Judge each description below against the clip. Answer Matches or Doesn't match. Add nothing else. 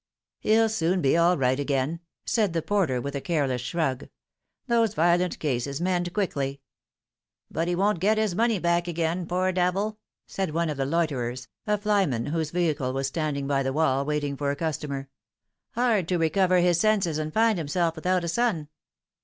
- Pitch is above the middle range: Doesn't match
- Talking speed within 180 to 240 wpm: Matches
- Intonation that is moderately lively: Matches